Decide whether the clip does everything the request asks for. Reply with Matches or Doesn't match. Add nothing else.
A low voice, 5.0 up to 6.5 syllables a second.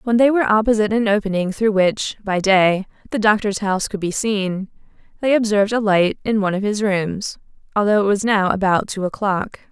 Doesn't match